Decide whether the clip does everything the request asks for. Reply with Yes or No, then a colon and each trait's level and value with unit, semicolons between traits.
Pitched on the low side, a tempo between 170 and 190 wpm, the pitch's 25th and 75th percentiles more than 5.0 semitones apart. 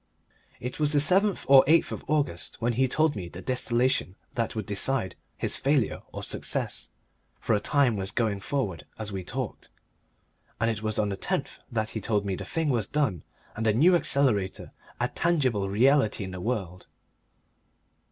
Yes: low, 115 Hz; average, 180 wpm; wide, 5.6 semitones